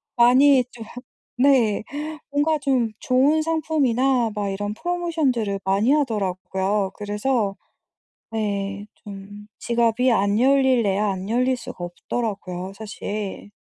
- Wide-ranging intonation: No, average, 4.6 semitones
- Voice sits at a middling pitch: No, high, 225 Hz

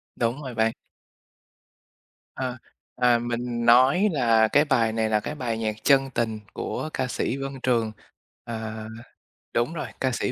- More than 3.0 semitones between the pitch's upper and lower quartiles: No, average, 2.7 semitones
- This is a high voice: No, low, 120 Hz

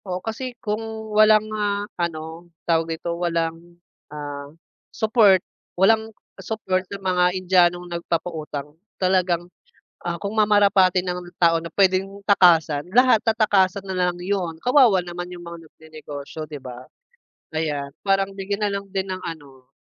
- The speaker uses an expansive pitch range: No, average, 3.3 semitones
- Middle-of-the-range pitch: Yes, medium, 180 Hz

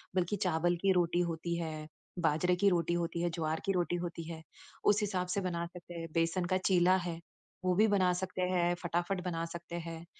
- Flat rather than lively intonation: Yes, narrow, 1.6 semitones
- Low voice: No, medium, 175 Hz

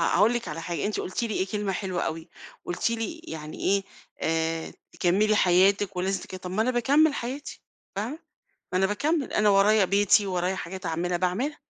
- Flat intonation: No, average, 3.8 semitones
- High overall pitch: Yes, high, 195 Hz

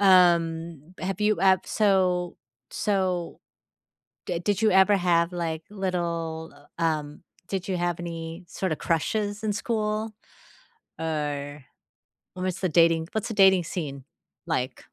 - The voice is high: No, medium, 175 Hz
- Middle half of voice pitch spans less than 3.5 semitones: Yes, average, 2.9 semitones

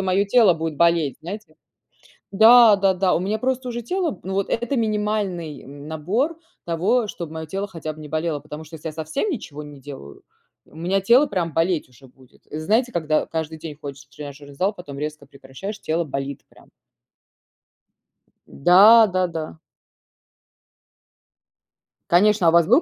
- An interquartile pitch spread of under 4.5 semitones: No, wide, 5.4 semitones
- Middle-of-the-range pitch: Yes, medium, 170 Hz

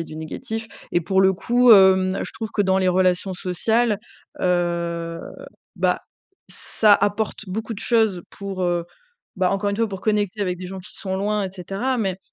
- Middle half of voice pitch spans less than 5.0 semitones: Yes, average, 2.7 semitones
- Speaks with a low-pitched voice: No, high, 190 Hz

